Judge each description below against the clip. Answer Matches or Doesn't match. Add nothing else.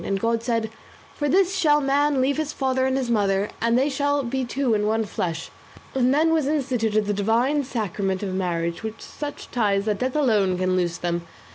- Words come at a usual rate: Doesn't match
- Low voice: Doesn't match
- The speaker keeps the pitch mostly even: Doesn't match